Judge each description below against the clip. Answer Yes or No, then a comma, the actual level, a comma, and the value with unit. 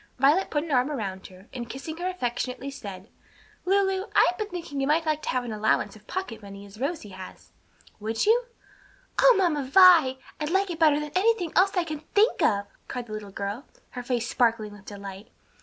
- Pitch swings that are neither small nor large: No, wide, 8.4 semitones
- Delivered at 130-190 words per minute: No, fast, 205 wpm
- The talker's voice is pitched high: Yes, very high, 275 Hz